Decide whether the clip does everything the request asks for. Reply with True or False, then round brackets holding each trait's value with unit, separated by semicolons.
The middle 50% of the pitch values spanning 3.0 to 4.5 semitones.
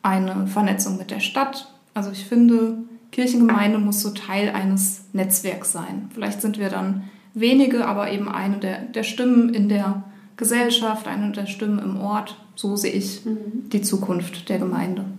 False (2.4 semitones)